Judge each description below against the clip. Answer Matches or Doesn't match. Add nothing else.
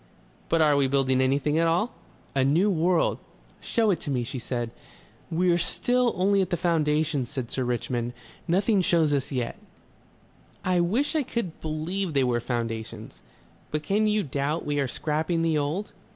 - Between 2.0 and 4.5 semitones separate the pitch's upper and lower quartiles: Doesn't match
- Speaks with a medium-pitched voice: Matches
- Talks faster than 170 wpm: Doesn't match